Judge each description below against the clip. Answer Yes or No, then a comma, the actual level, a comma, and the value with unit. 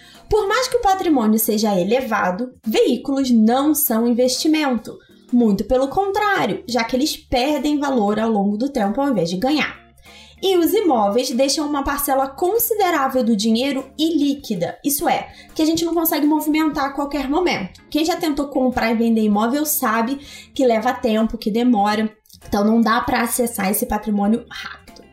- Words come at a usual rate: Yes, average, 165 wpm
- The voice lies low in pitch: No, very high, 260 Hz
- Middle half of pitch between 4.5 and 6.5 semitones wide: Yes, average, 4.8 semitones